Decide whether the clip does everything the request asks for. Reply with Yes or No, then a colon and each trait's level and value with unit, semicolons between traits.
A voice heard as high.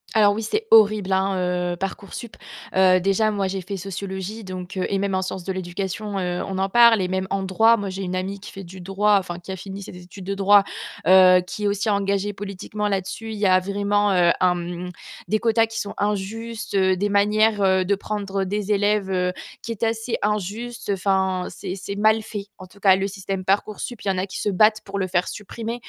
Yes: high, 195 Hz